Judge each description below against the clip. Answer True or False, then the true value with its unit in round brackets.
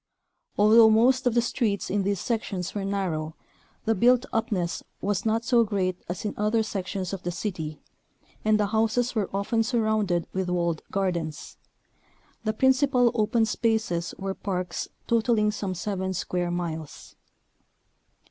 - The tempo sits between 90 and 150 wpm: True (145 wpm)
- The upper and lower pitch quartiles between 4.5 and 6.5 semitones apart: False (3.6 semitones)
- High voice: True (205 Hz)